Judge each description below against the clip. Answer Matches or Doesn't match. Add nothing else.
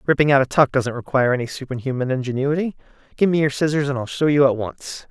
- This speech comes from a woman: Doesn't match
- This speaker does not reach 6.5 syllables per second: Doesn't match